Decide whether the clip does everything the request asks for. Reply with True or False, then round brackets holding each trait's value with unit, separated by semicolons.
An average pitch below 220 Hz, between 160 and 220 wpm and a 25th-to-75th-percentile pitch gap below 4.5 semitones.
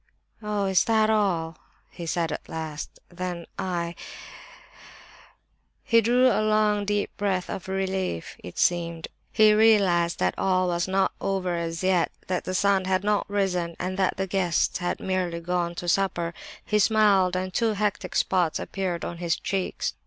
True (185 Hz; 165 wpm; 2.8 semitones)